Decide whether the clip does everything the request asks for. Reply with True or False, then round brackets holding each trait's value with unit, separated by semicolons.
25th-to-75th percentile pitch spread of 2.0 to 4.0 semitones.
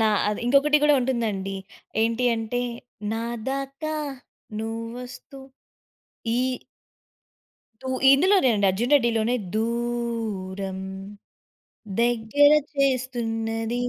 True (2.9 semitones)